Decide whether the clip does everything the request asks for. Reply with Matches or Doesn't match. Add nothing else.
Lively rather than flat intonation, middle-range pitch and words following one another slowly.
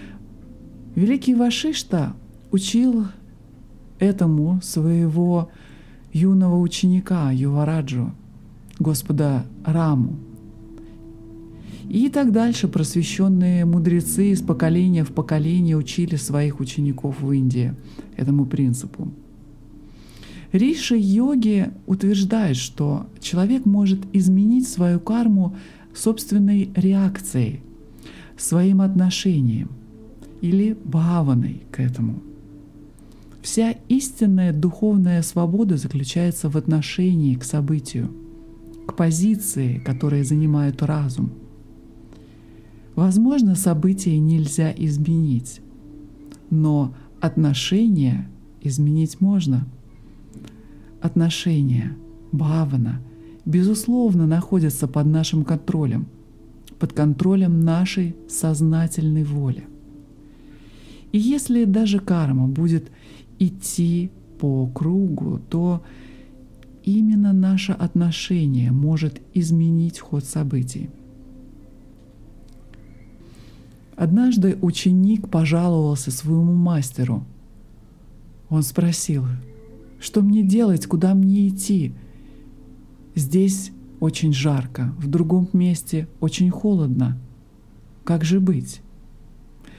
Matches